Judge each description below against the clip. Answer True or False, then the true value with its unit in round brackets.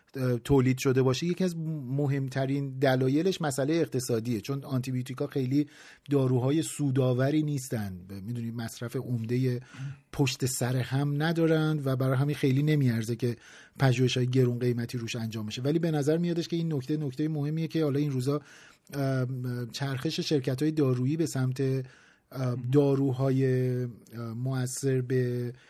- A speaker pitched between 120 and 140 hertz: True (135 Hz)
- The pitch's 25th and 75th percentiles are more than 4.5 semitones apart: False (2.5 semitones)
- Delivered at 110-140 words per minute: True (130 wpm)